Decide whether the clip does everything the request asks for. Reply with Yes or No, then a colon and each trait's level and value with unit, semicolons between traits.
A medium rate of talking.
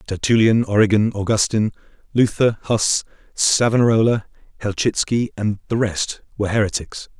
No: slow, 100 wpm